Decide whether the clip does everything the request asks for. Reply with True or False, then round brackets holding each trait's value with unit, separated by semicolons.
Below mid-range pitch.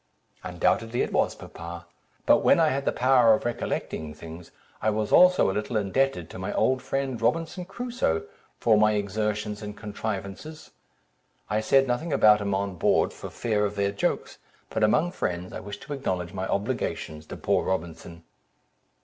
True (105 Hz)